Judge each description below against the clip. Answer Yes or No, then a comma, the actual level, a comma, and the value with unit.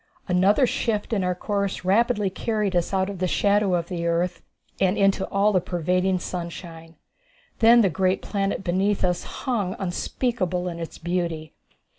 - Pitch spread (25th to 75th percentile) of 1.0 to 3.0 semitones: Yes, narrow, 2.5 semitones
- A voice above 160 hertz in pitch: Yes, medium, 185 Hz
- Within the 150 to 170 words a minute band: Yes, average, 160 wpm